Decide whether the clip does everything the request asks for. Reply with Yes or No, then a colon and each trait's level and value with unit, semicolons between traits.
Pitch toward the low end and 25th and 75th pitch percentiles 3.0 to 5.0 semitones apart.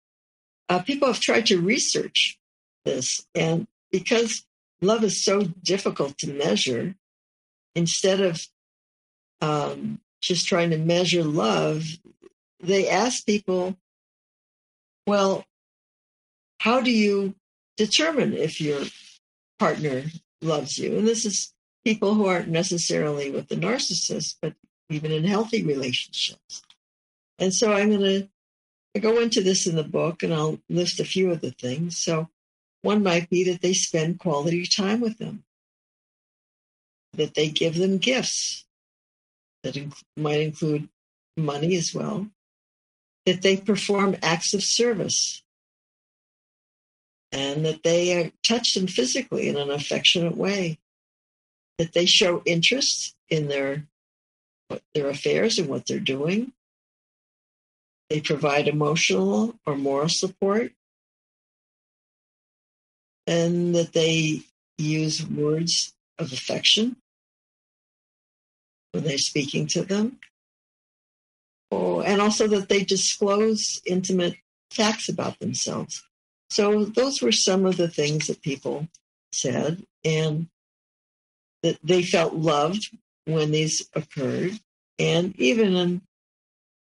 No: medium, 180 Hz; average, 4.7 semitones